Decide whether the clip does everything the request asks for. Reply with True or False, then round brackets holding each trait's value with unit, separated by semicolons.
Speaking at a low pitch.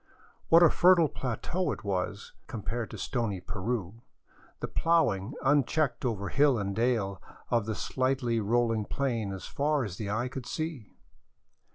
True (120 Hz)